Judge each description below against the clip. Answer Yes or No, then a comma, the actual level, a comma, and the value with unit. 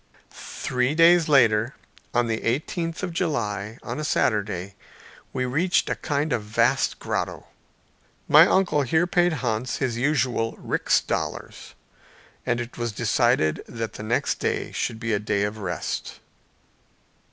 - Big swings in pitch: Yes, wide, 5.9 semitones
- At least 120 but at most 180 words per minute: Yes, average, 145 wpm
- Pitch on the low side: Yes, low, 120 Hz